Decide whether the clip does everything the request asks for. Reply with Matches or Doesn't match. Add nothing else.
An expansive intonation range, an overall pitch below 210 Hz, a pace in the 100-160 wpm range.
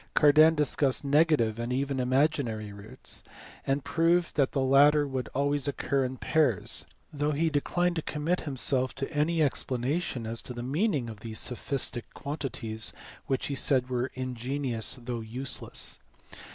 Doesn't match